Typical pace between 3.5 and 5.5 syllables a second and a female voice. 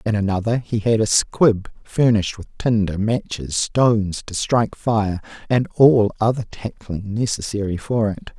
No: 4.5 syllables/s; male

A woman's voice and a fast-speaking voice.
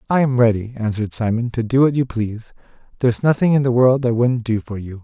No: male; fast, 240 wpm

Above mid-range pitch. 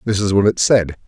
No: low, 100 Hz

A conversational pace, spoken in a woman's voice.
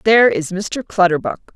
Yes: average, 155 wpm; female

